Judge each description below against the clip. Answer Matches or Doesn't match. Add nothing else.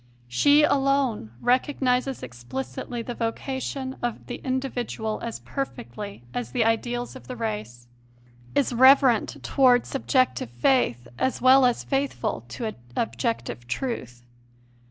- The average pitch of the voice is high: Matches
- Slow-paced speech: Matches